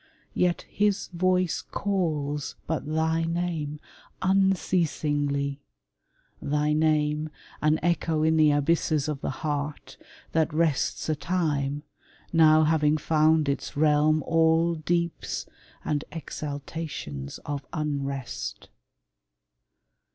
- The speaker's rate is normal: No, slow, 100 wpm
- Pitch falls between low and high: Yes, medium, 155 Hz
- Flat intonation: Yes, narrow, 2.0 semitones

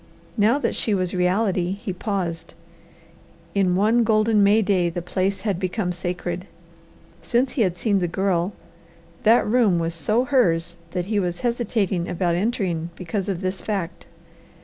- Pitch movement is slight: No, average, 3.4 semitones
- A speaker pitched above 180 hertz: Yes, high, 190 Hz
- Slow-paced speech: No, average, 155 wpm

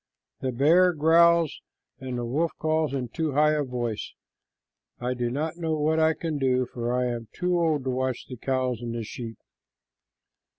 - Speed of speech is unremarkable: Yes, average, 170 wpm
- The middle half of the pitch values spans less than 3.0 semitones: No, average, 4.4 semitones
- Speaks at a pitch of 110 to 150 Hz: Yes, low, 135 Hz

